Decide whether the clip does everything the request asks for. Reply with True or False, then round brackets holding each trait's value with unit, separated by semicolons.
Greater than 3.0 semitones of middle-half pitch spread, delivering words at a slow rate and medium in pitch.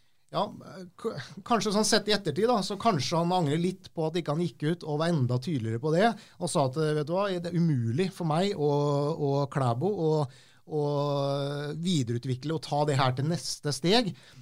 False (4.1 semitones; 205 wpm; 155 Hz)